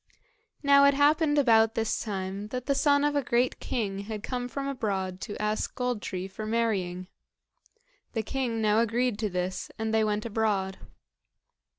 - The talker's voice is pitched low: No, high, 220 Hz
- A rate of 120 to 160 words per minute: No, average, 170 wpm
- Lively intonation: No, average, 3.7 semitones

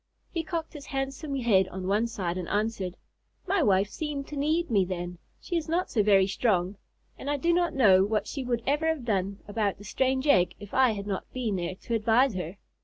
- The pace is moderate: No, fast, 220 wpm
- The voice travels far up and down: Yes, wide, 6.4 semitones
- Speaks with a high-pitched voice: Yes, high, 225 Hz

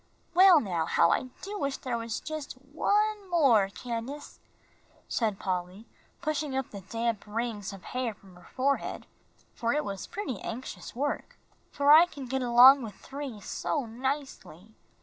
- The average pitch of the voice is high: Yes, very high, 255 Hz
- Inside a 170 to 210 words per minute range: No, average, 155 wpm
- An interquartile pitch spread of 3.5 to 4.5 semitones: No, average, 5.2 semitones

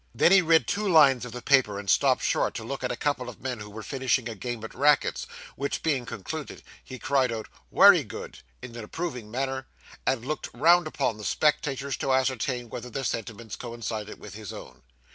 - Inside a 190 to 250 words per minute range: Yes, fast, 205 wpm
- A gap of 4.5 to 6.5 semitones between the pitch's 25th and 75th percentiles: No, average, 3.7 semitones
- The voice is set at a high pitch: No, low, 125 Hz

